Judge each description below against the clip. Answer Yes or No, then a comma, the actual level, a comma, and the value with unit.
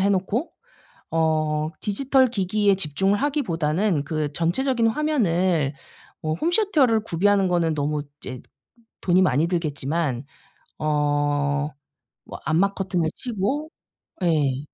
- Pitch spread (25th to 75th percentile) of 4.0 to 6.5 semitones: Yes, wide, 5.5 semitones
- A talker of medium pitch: Yes, medium, 175 Hz